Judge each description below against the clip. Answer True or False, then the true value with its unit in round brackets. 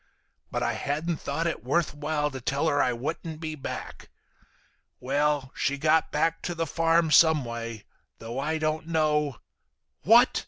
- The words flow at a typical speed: True (160 wpm)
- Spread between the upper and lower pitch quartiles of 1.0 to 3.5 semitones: True (2.6 semitones)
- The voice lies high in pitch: False (150 Hz)